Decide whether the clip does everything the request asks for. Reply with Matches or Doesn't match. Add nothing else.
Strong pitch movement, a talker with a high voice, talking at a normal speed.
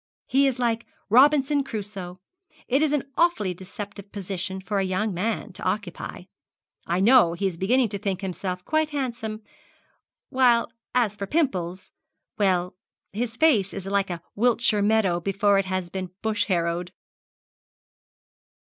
Doesn't match